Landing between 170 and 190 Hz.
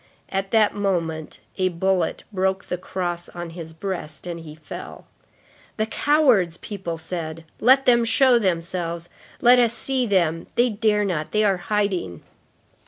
Yes: medium, 185 Hz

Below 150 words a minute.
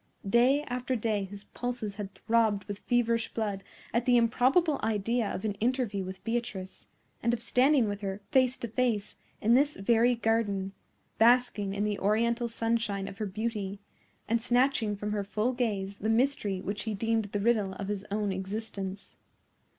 No: average, 170 wpm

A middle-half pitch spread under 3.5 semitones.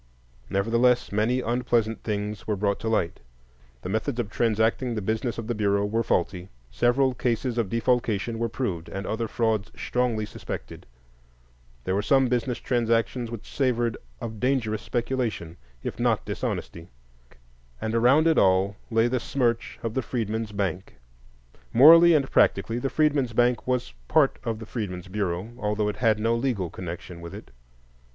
Yes: average, 3.1 semitones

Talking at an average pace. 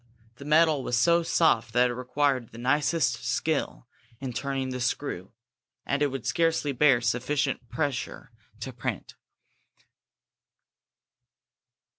No: slow, 120 wpm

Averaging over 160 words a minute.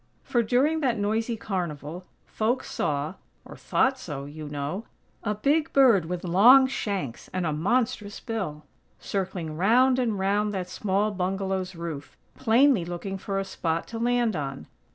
No: average, 155 wpm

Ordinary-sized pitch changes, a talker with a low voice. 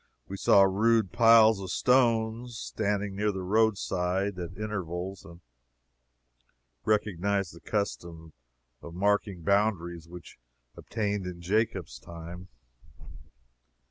Yes: average, 3.3 semitones; low, 100 Hz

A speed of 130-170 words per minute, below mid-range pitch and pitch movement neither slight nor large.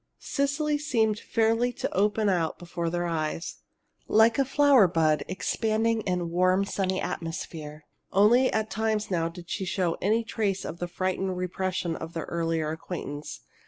No: average, 155 wpm; medium, 185 Hz; average, 4.6 semitones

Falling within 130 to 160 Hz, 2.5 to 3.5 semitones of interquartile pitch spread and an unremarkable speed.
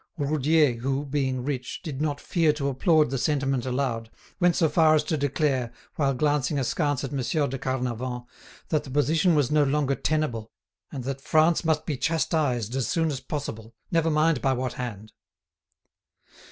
Yes: medium, 140 Hz; average, 3.1 semitones; average, 170 wpm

